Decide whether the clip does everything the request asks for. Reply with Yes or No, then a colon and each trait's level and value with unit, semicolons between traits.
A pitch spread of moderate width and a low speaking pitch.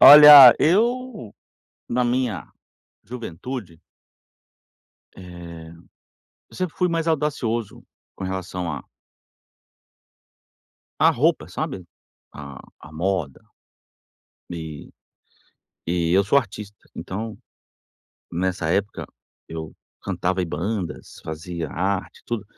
No: wide, 6.6 semitones; very low, 95 Hz